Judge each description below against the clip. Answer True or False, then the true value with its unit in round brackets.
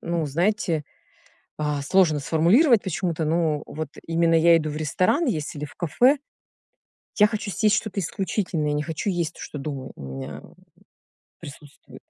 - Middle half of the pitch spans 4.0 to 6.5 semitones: True (4.3 semitones)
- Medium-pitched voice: True (165 Hz)